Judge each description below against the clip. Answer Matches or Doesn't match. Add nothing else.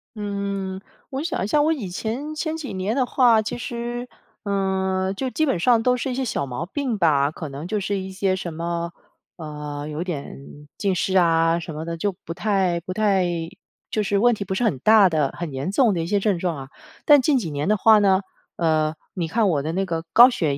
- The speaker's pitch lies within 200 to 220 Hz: Doesn't match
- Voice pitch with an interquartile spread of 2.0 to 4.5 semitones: Doesn't match